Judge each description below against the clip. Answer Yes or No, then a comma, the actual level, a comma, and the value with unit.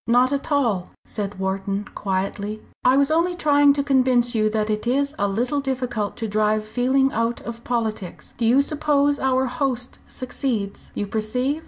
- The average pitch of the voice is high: Yes, high, 245 Hz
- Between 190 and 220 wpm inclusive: No, average, 170 wpm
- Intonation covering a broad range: No, average, 4.3 semitones